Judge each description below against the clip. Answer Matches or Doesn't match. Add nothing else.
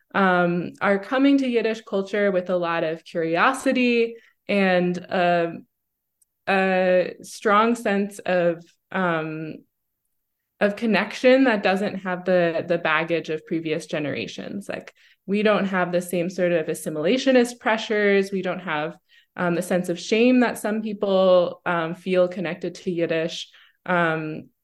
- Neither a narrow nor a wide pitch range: Matches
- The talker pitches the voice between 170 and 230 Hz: Matches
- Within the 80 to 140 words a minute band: Matches